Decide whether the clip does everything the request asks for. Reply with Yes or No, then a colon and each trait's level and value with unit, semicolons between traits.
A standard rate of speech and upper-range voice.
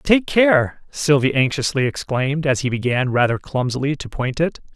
No: average, 165 wpm; medium, 140 Hz